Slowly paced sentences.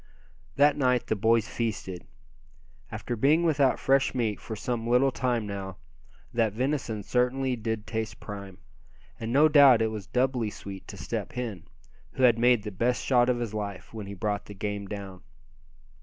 No: average, 170 wpm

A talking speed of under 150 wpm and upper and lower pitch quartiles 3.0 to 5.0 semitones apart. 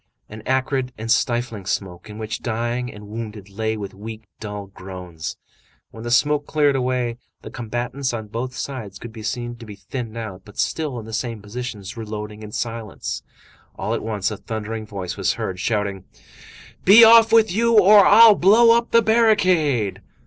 No: average, 180 wpm; average, 4.2 semitones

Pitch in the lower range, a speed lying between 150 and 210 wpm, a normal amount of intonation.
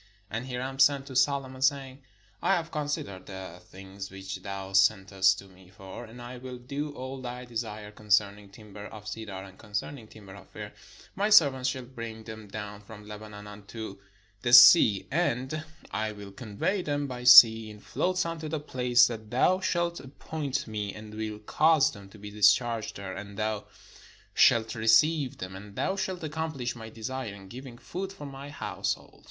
Yes: low, 115 Hz; average, 180 wpm; average, 4.8 semitones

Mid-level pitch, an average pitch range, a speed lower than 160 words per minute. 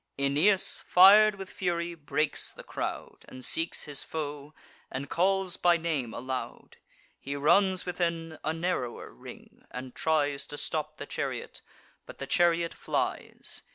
Yes: medium, 160 Hz; average, 3.8 semitones; average, 140 wpm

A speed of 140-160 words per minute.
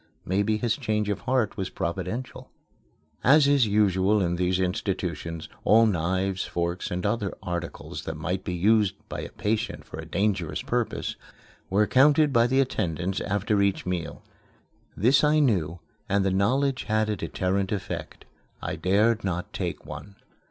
Yes: average, 155 wpm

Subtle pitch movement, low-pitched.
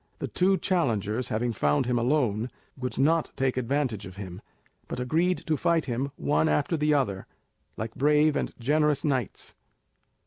No: average, 4.8 semitones; low, 130 Hz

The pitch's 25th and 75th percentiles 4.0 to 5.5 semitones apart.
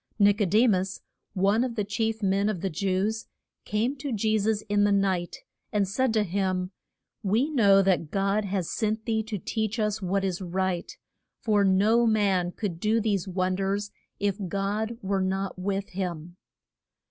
No: narrow, 2.4 semitones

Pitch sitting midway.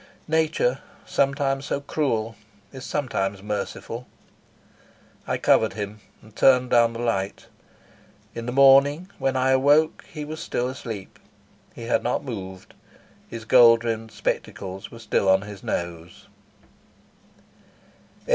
No: low, 120 Hz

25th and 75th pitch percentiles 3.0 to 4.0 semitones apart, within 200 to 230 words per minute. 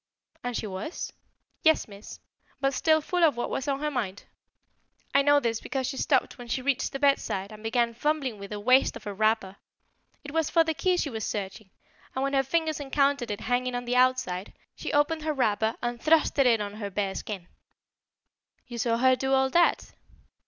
No: average, 4.6 semitones; fast, 205 wpm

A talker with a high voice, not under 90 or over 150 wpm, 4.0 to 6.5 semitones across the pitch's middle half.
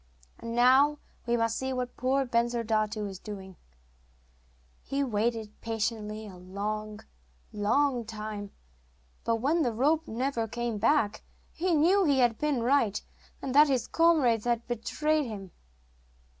Yes: high, 235 Hz; slow, 135 wpm; average, 4.3 semitones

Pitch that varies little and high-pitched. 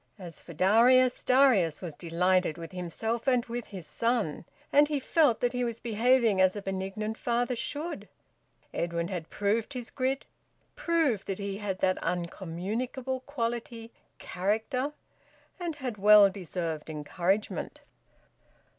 No: average, 5.2 semitones; high, 215 Hz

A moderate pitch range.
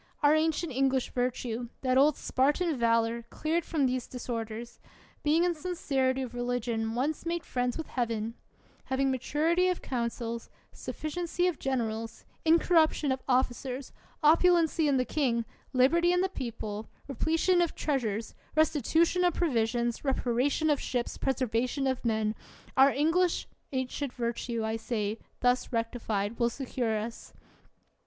Yes: average, 4.8 semitones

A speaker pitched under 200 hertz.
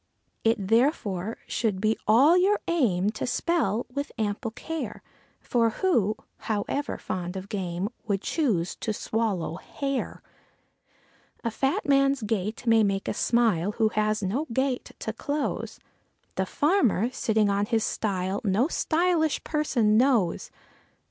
No: high, 225 Hz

